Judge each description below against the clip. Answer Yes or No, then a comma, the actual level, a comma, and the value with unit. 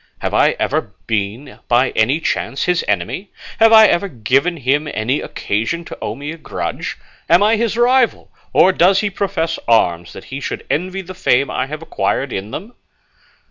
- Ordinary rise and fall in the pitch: No, wide, 7.6 semitones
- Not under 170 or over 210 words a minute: Yes, average, 180 wpm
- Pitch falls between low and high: Yes, medium, 155 Hz